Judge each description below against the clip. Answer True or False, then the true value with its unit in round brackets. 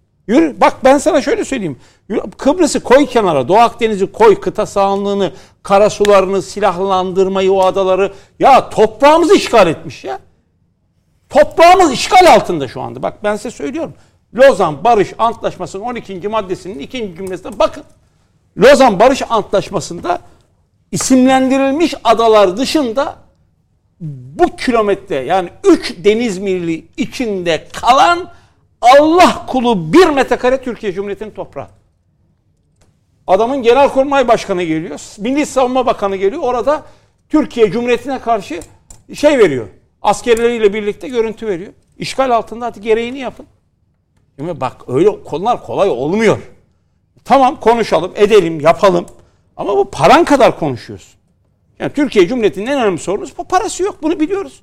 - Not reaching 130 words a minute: True (120 wpm)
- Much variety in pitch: True (6.1 semitones)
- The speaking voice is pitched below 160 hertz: False (225 Hz)